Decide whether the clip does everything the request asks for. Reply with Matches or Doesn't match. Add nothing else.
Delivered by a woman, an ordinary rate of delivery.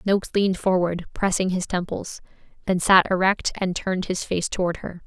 Matches